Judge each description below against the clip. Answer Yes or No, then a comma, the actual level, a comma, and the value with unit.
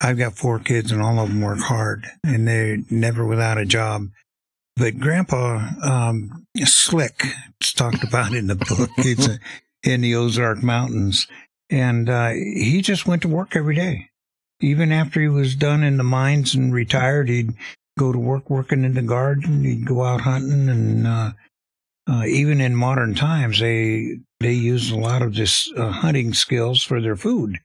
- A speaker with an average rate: Yes, average, 180 wpm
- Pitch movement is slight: No, average, 3.1 semitones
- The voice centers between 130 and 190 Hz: No, low, 120 Hz